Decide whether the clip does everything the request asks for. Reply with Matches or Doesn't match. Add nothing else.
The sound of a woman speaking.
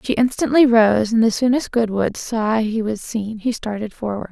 Matches